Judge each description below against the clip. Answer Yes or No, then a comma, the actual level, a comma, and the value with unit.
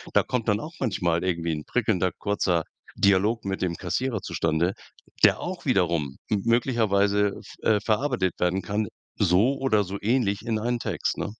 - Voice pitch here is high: No, low, 100 Hz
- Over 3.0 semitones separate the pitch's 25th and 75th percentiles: Yes, average, 4.0 semitones